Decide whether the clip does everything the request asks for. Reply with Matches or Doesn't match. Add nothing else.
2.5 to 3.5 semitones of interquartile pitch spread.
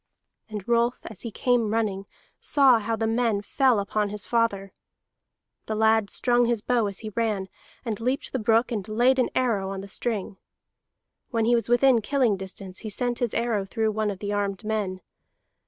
Matches